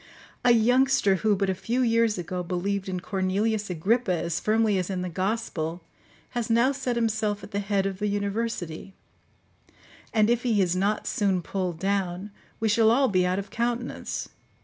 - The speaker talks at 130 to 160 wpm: No, average, 175 wpm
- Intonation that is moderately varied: Yes, average, 3.4 semitones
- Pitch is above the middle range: Yes, high, 200 Hz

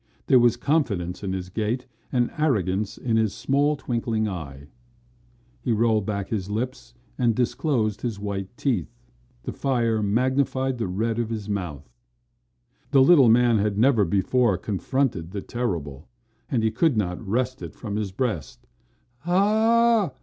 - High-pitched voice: No, low, 115 Hz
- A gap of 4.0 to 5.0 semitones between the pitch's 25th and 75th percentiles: Yes, average, 4.4 semitones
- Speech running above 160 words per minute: No, average, 150 wpm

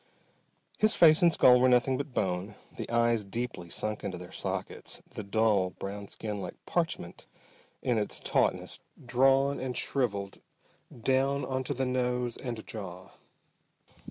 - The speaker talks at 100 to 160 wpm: Yes, average, 140 wpm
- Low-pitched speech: Yes, low, 120 Hz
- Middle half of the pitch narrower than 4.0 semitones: No, average, 4.4 semitones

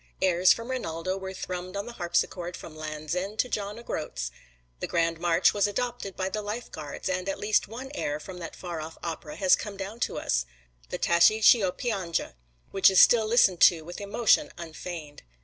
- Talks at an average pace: Yes, average, 195 wpm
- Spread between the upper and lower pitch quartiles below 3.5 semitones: No, average, 3.8 semitones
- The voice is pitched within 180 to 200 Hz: Yes, medium, 185 Hz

